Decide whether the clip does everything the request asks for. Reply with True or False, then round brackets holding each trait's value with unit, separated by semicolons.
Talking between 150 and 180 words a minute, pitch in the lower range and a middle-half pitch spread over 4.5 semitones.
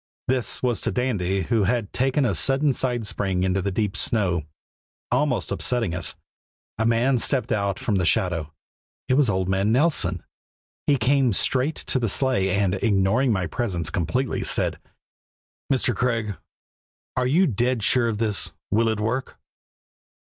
True (155 wpm; 115 Hz; 4.9 semitones)